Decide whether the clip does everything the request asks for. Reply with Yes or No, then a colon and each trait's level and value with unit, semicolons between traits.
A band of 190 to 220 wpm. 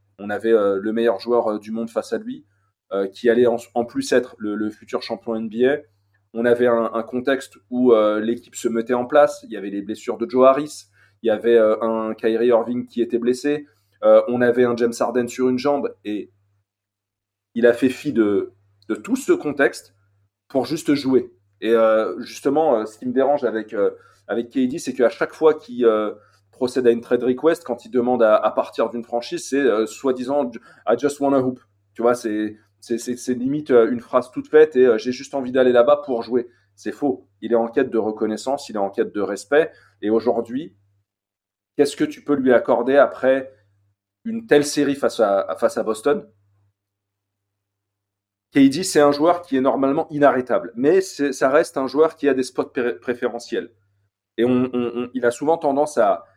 Yes: average, 210 wpm